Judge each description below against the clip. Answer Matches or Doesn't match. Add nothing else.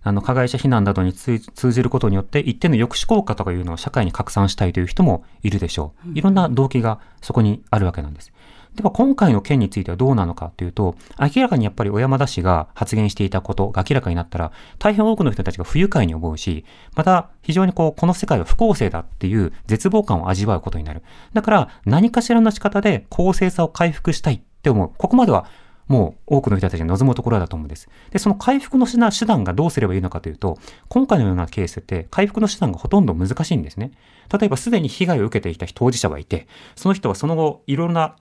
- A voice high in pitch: Doesn't match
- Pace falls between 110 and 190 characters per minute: Doesn't match